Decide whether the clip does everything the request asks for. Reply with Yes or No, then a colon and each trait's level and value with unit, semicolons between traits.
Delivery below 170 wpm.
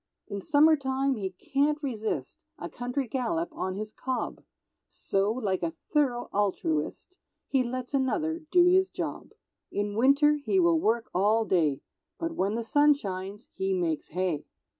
Yes: average, 150 wpm